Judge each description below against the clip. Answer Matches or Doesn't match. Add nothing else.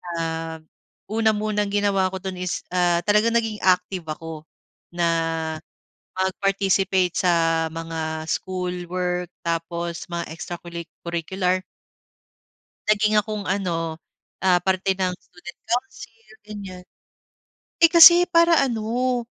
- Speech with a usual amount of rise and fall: Matches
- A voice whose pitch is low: Doesn't match